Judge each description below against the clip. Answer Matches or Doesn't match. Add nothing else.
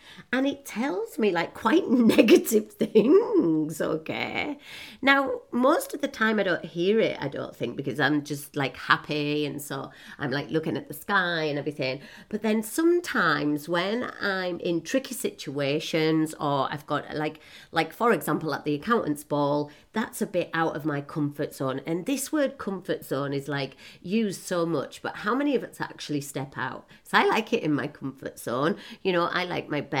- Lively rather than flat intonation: Matches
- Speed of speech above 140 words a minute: Matches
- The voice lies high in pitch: Doesn't match